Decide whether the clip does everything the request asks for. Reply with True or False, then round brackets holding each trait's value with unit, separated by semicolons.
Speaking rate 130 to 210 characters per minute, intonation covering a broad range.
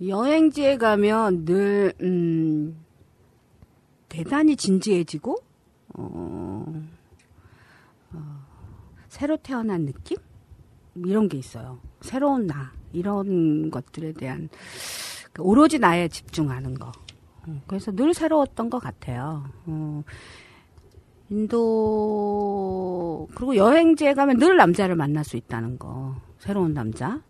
True (205 characters per minute; 8.4 semitones)